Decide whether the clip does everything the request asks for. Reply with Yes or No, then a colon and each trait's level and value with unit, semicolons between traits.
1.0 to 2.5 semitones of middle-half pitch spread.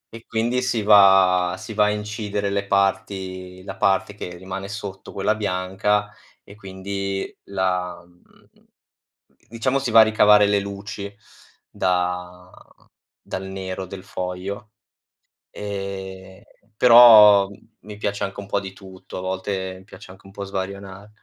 Yes: narrow, 1.7 semitones